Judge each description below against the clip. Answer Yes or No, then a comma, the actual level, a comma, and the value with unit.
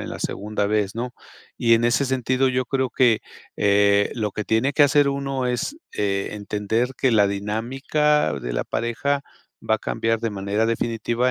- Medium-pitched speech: No, low, 115 Hz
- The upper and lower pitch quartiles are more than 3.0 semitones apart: Yes, average, 3.9 semitones